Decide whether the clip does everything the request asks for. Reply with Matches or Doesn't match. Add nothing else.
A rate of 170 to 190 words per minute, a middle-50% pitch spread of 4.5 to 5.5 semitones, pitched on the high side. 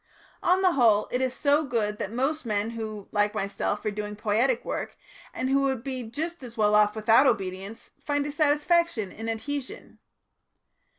Matches